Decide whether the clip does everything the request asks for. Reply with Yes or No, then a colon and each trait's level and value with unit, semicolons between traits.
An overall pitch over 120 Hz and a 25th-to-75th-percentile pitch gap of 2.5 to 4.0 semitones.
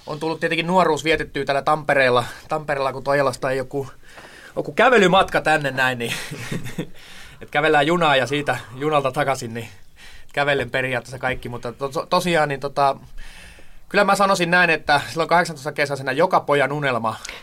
Yes: medium, 140 Hz; average, 2.9 semitones